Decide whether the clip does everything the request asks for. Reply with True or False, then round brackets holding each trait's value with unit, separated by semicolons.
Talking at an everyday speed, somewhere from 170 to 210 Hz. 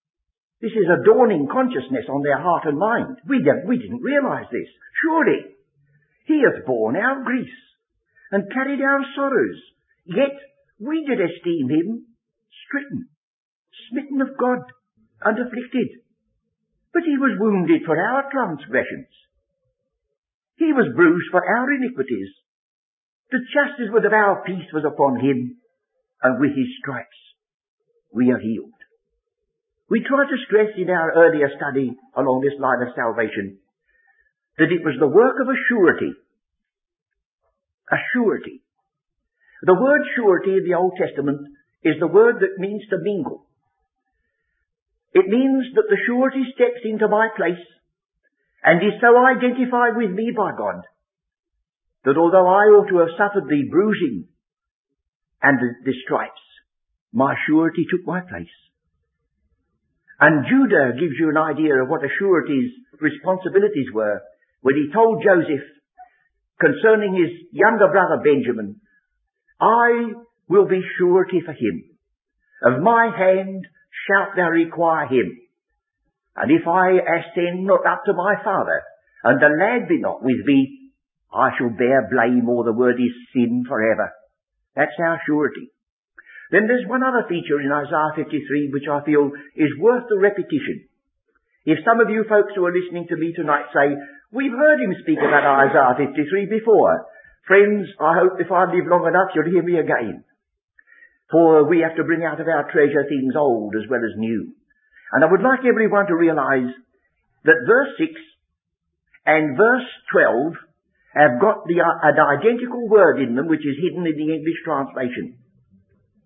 True (150 wpm; 190 Hz)